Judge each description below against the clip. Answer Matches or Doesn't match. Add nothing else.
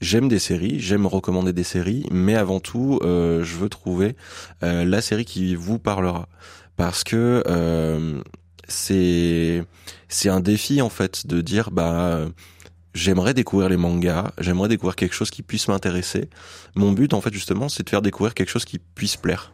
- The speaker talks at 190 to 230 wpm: Doesn't match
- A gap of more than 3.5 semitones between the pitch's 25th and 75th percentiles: Doesn't match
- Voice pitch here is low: Matches